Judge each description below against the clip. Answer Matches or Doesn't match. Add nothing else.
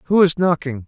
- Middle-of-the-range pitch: Matches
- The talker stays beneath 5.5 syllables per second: Doesn't match